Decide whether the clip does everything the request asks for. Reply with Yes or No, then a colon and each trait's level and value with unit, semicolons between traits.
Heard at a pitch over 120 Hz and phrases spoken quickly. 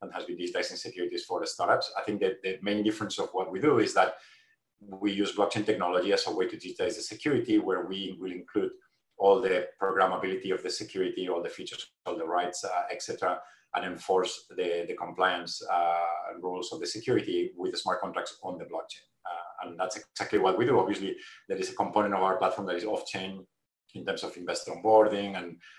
No: low, 105 Hz; fast, 210 wpm